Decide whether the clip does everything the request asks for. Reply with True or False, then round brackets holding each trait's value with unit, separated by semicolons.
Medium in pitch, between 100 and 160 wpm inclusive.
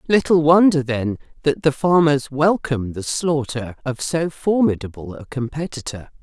True (145 Hz; 135 wpm)